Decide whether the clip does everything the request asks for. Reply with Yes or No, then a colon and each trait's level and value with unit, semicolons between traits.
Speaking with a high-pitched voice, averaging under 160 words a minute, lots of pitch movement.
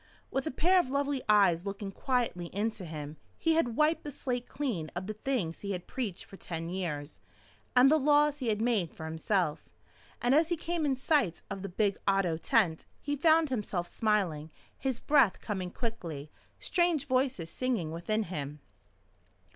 No: high, 215 Hz; average, 175 wpm; wide, 7.7 semitones